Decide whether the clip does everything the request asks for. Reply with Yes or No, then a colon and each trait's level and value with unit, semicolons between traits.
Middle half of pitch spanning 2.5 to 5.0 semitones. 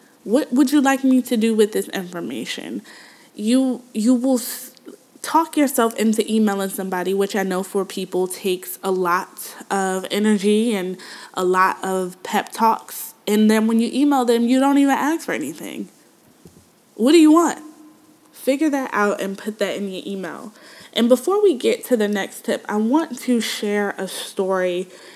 No: wide, 5.5 semitones